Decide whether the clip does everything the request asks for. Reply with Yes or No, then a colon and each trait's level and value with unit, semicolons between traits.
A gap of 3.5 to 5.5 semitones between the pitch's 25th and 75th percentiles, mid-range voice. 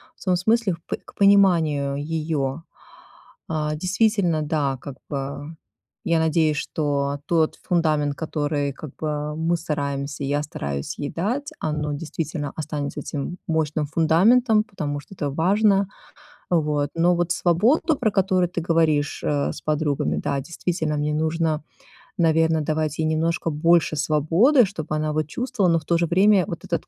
No: average, 2.8 semitones; medium, 160 Hz